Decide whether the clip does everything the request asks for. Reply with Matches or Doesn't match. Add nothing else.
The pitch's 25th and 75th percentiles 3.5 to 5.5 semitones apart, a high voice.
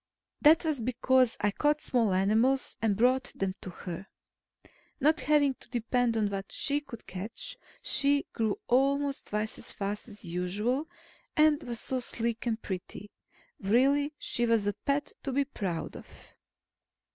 Matches